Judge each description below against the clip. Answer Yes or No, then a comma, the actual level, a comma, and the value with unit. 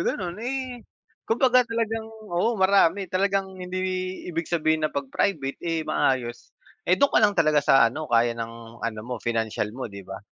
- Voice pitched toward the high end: No, medium, 165 Hz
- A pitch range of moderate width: No, wide, 9.0 semitones